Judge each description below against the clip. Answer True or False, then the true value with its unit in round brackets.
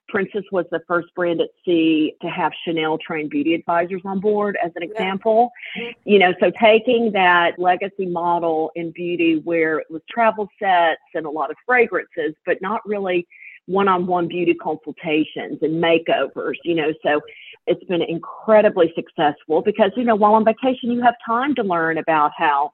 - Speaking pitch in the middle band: True (180 Hz)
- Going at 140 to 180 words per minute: True (175 wpm)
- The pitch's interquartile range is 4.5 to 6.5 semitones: True (4.9 semitones)